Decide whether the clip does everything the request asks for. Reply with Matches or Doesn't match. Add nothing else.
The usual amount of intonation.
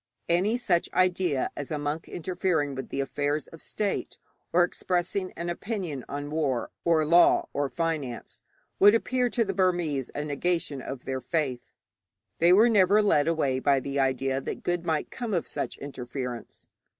Matches